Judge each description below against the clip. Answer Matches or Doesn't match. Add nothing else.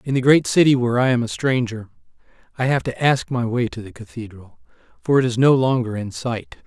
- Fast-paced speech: Matches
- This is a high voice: Doesn't match